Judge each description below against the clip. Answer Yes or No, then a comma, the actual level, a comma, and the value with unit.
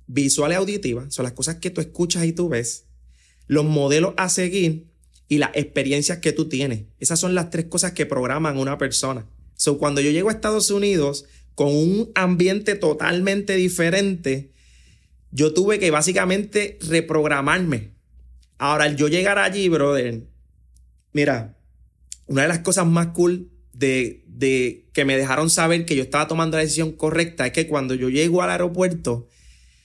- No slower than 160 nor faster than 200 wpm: Yes, average, 165 wpm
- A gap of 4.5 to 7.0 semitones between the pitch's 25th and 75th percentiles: Yes, average, 5.0 semitones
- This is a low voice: No, medium, 150 Hz